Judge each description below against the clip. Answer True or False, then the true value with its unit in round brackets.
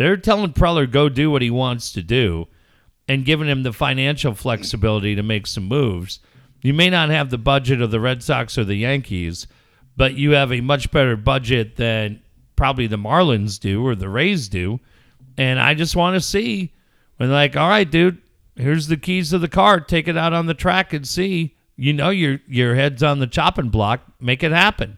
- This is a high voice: False (135 Hz)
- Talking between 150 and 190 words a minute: False (205 wpm)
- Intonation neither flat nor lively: False (6.0 semitones)